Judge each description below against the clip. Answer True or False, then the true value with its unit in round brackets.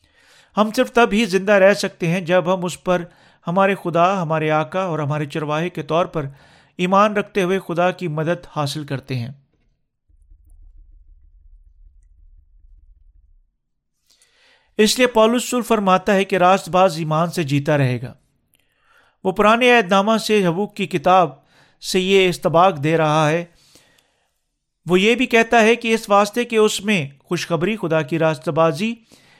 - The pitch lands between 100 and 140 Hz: False (175 Hz)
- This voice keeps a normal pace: True (150 wpm)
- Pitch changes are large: True (5.7 semitones)